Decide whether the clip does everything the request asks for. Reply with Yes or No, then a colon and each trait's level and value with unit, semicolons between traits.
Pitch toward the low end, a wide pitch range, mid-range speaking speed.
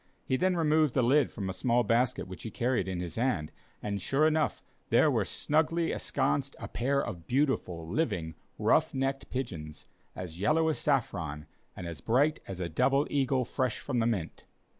Yes: low, 125 Hz; wide, 7.3 semitones; average, 180 wpm